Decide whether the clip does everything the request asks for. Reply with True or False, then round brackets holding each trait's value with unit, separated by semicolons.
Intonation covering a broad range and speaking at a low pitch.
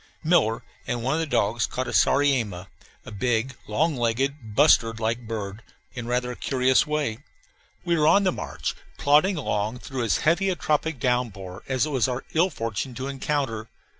False (4.6 semitones; 125 Hz)